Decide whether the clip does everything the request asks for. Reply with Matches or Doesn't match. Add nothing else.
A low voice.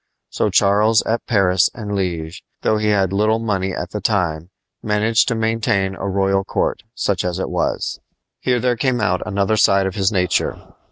Matches